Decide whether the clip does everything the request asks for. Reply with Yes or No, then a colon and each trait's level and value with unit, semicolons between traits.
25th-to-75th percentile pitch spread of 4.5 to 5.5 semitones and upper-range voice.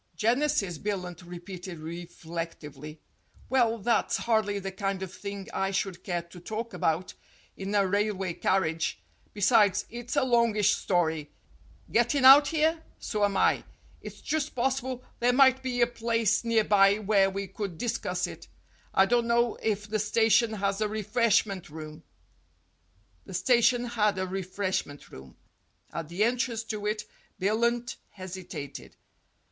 No: average, 4.0 semitones; high, 205 Hz